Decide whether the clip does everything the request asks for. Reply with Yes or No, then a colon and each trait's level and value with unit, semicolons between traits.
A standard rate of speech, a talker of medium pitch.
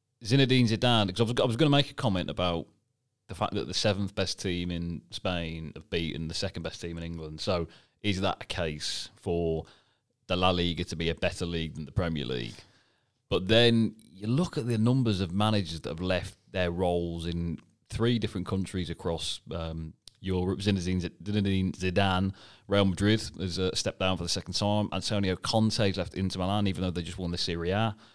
No: average, 195 wpm; very low, 95 Hz